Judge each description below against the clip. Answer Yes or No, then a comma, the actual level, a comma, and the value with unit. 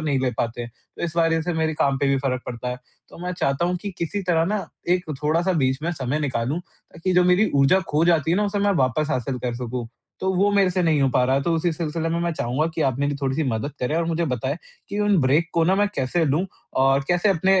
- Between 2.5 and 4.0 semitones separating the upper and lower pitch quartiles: No, average, 4.7 semitones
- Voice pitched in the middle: Yes, medium, 160 Hz